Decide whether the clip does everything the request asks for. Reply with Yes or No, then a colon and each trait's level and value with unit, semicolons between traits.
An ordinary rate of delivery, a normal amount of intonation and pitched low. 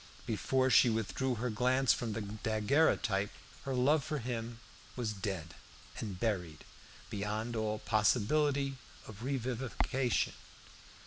No: slow, 115 wpm; average, 3.5 semitones; low, 115 Hz